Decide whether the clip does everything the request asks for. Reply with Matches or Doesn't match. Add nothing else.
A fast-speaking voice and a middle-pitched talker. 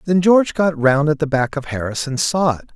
Matches